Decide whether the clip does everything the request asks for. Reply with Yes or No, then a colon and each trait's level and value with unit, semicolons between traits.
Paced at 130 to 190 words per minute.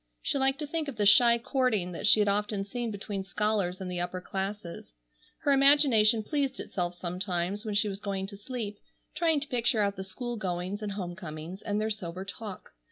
No: fast, 205 wpm